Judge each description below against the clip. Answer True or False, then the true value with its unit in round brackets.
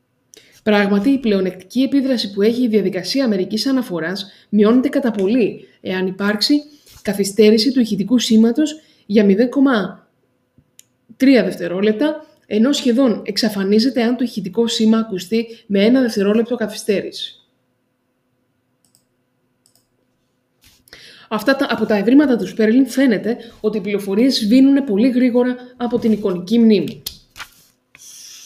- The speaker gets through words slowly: True (110 wpm)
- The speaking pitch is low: False (220 Hz)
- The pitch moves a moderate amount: True (4.2 semitones)